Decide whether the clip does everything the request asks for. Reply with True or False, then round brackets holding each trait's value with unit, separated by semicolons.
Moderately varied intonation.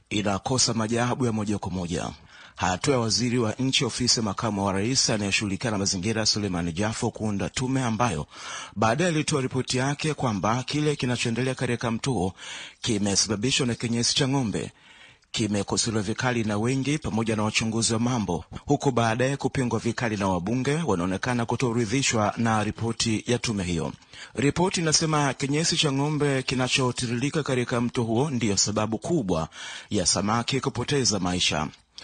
True (3.6 semitones)